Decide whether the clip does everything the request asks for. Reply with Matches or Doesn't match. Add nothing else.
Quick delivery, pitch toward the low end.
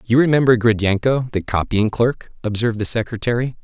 Doesn't match